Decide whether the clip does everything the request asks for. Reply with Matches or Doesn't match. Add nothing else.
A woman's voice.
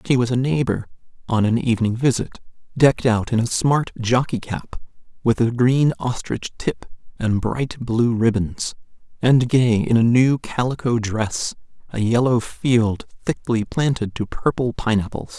Doesn't match